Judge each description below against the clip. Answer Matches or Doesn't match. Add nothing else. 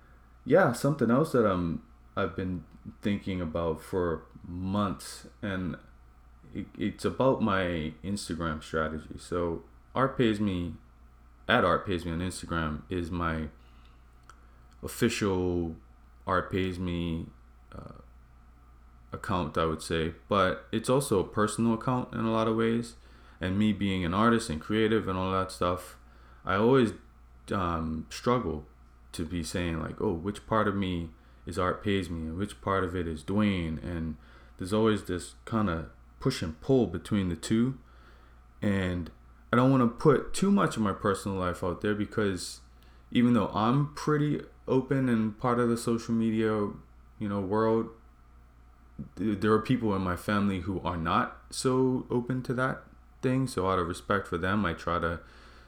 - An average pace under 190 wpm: Matches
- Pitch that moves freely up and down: Matches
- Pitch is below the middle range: Matches